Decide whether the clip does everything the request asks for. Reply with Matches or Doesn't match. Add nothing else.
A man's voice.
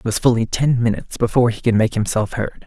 Matches